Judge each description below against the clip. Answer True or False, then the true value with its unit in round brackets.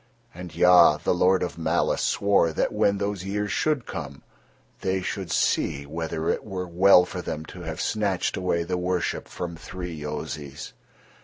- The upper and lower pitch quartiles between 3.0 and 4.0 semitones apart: False (2.6 semitones)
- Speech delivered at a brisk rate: False (165 wpm)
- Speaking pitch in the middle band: False (90 Hz)